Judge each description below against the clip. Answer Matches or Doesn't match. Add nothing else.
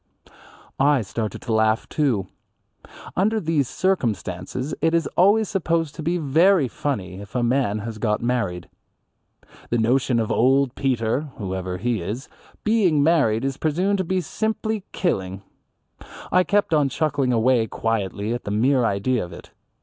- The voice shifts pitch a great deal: Matches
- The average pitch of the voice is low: Matches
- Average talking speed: Matches